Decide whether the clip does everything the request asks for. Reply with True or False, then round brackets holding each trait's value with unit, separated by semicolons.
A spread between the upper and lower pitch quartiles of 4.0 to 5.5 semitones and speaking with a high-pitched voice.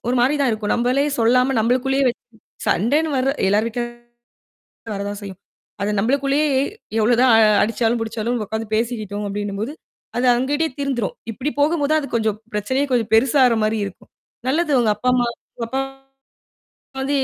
False (3.5 semitones; 245 Hz)